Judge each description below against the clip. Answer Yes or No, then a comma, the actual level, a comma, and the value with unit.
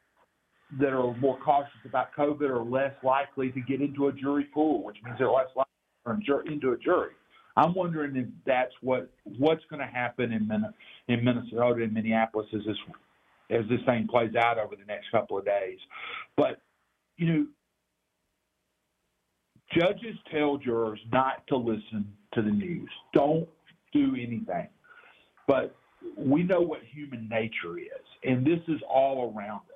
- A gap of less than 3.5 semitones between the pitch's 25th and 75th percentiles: No, average, 4.5 semitones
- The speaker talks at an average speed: Yes, average, 160 wpm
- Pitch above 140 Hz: No, low, 135 Hz